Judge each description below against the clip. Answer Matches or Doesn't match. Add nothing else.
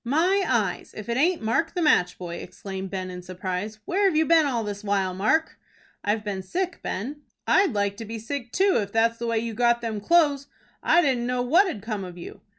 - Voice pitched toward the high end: Matches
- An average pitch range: Doesn't match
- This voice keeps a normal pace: Doesn't match